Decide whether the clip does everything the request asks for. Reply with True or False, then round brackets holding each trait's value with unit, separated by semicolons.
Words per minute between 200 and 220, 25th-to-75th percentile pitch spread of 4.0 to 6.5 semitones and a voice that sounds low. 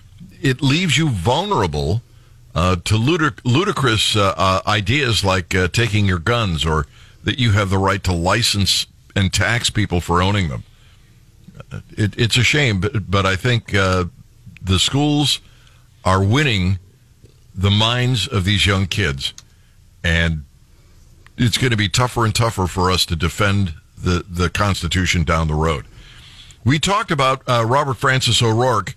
False (155 wpm; 4.5 semitones; 105 Hz)